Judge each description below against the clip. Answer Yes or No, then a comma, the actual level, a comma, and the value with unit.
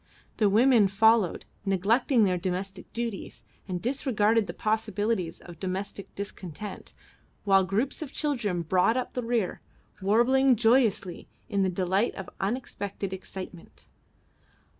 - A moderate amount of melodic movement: Yes, average, 3.6 semitones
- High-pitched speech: Yes, high, 205 Hz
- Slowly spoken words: Yes, slow, 120 wpm